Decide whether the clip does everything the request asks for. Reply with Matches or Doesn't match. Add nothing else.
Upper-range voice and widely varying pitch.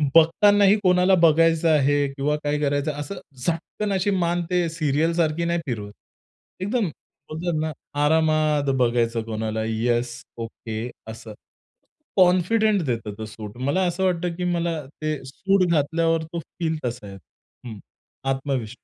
Doesn't match